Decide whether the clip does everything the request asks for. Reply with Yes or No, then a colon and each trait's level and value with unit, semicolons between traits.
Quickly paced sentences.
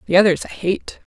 Yes: fast, 210 wpm